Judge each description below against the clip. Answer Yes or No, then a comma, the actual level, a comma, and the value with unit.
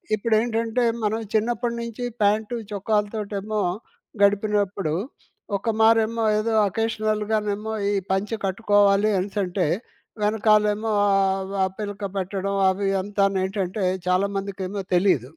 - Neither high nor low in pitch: No, high, 205 Hz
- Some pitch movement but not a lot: No, narrow, 1.9 semitones